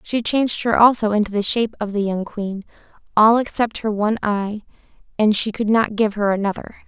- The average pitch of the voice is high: Yes, high, 215 Hz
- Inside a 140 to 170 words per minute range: No, average, 200 wpm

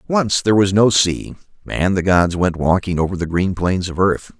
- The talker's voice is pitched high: No, very low, 95 Hz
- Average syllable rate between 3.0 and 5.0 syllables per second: Yes, 4.9 syllables/s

